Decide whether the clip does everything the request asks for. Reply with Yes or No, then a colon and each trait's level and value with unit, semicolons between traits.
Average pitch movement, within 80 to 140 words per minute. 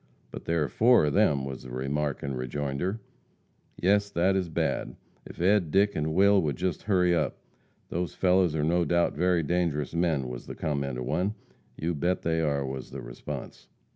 No: average, 4.4 semitones; average, 190 wpm